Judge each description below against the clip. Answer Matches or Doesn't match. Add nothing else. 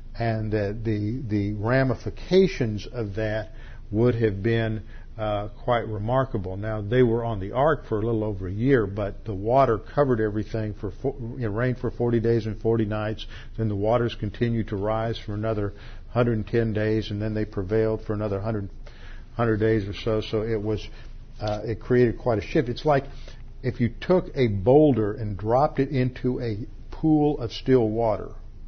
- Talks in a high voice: Doesn't match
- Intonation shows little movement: Matches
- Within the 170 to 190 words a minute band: Matches